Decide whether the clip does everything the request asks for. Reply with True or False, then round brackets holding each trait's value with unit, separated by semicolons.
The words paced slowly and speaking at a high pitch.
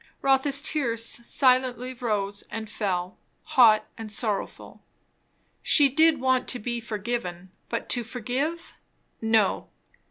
True (115 wpm; 235 Hz)